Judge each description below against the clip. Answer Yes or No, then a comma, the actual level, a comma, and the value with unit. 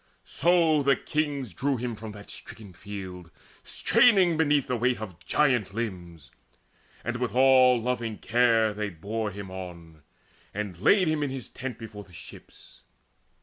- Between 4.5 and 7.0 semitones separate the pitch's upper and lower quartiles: Yes, average, 5.1 semitones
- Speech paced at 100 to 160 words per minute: Yes, average, 150 wpm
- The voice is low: Yes, low, 115 Hz